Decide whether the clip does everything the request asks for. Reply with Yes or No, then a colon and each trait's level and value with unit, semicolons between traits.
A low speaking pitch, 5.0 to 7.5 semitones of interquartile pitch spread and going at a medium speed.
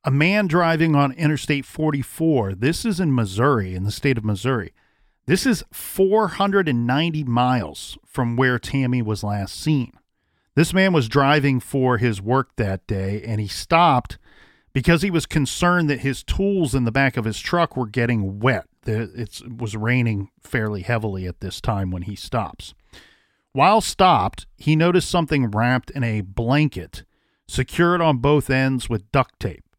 Yes: low, 130 Hz; wide, 5.5 semitones; average, 160 wpm